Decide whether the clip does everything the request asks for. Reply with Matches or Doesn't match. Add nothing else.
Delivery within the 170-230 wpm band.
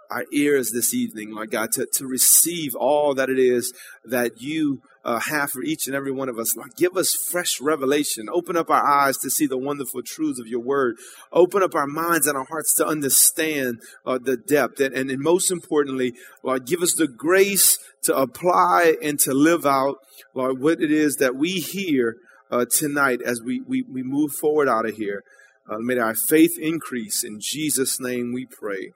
Matches